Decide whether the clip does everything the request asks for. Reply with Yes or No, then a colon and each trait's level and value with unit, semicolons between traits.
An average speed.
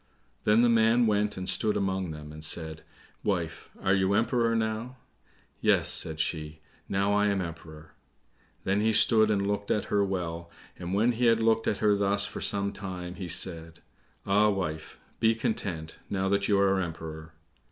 Yes: average, 175 wpm